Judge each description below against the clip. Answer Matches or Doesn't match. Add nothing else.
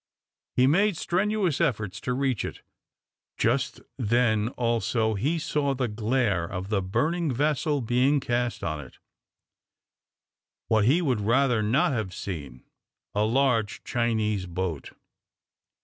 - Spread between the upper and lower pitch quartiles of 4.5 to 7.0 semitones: Matches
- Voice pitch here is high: Doesn't match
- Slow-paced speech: Matches